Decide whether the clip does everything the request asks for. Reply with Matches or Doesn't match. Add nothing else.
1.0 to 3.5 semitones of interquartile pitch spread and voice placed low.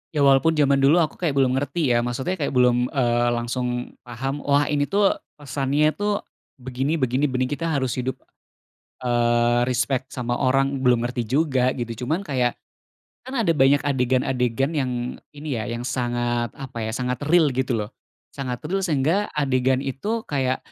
Matches